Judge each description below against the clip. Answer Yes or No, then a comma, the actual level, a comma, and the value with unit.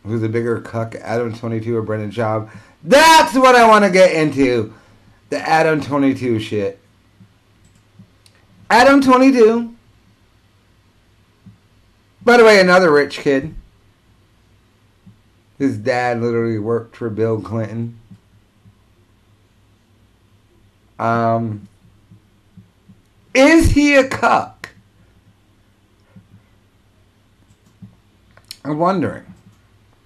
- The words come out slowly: Yes, slow, 90 wpm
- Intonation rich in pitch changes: No, average, 2.7 semitones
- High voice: No, low, 110 Hz